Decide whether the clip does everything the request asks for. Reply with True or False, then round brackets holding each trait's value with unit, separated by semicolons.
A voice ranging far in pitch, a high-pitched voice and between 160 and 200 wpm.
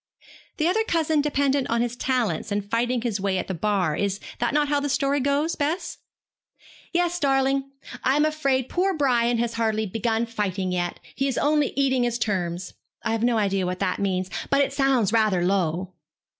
True (5.9 semitones; 240 Hz; 190 wpm)